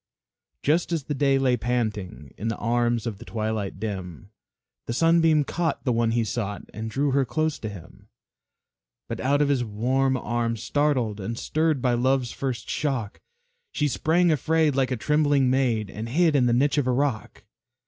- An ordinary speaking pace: Yes, average, 180 wpm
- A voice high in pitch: No, low, 125 Hz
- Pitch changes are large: No, average, 4.2 semitones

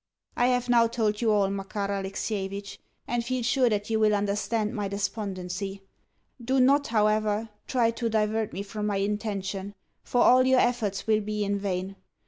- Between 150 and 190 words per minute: Yes, average, 170 wpm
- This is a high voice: Yes, high, 210 Hz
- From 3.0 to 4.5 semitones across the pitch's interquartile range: No, narrow, 2.5 semitones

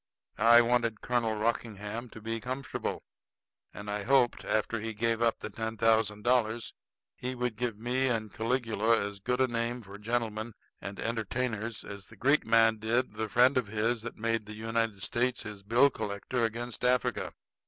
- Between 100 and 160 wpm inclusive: No, average, 175 wpm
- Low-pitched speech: Yes, low, 115 Hz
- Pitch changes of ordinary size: No, narrow, 2.1 semitones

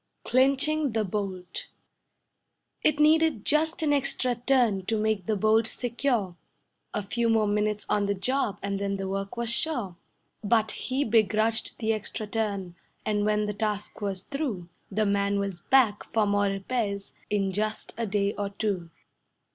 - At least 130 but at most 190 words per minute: Yes, average, 160 wpm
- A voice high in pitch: Yes, high, 215 Hz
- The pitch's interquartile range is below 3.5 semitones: Yes, average, 3.1 semitones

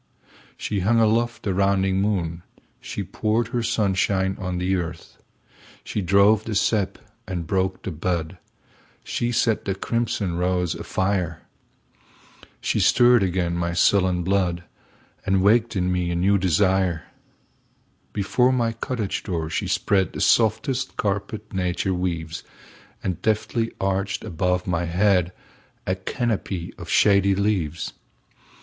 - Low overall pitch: Yes, very low, 95 Hz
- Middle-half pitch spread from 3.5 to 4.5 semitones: No, average, 3.0 semitones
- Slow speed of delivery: Yes, slow, 110 wpm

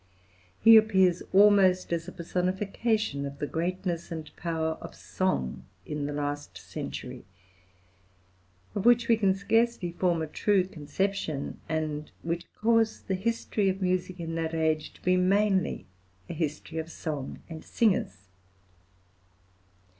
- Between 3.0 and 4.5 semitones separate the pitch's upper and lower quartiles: Yes, average, 3.8 semitones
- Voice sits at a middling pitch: Yes, medium, 180 Hz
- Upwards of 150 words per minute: No, slow, 135 wpm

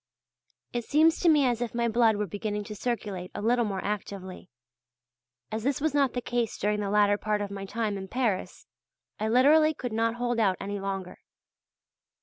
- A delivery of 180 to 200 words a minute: Yes, average, 190 wpm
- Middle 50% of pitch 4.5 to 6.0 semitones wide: No, average, 3.2 semitones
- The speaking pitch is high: Yes, high, 220 Hz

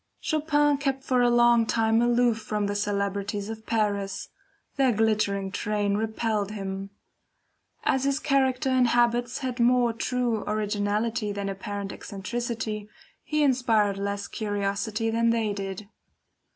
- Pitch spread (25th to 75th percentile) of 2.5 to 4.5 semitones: Yes, average, 3.1 semitones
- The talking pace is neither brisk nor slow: No, slow, 130 wpm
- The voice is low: No, high, 220 Hz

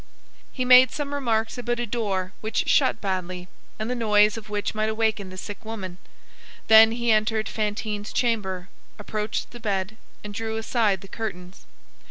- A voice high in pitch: Yes, high, 215 Hz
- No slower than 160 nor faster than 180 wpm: Yes, average, 165 wpm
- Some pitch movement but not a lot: No, narrow, 2.1 semitones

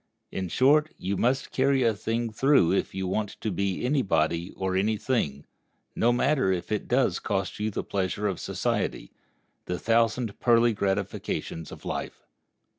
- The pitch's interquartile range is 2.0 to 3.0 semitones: No, average, 4.3 semitones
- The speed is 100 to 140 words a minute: No, average, 165 wpm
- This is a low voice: Yes, low, 105 Hz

